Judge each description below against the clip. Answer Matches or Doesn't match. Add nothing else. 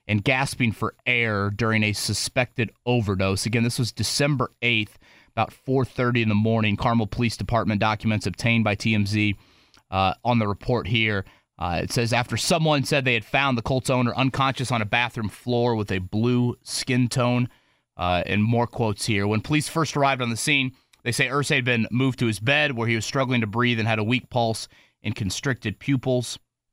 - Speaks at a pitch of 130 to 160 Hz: Doesn't match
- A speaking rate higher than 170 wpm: Matches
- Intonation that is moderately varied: Matches